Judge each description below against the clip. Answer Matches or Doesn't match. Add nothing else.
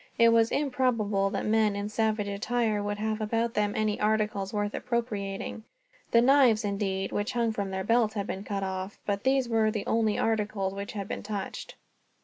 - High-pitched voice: Matches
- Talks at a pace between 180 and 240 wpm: Matches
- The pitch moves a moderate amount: Doesn't match